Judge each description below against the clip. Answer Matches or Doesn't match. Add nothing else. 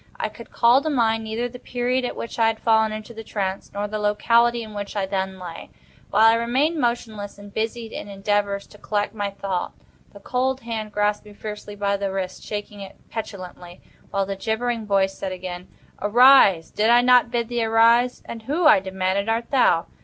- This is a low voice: Doesn't match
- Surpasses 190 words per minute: Matches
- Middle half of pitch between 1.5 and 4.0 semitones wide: Matches